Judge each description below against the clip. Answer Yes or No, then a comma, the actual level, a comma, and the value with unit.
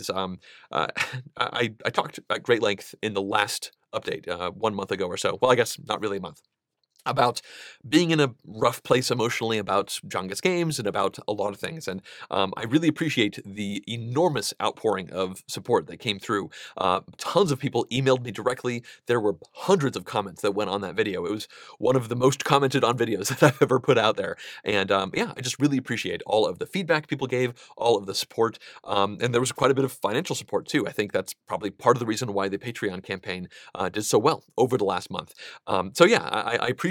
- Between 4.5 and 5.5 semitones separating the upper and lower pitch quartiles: Yes, average, 4.8 semitones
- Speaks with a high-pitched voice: No, low, 120 Hz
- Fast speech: Yes, fast, 230 wpm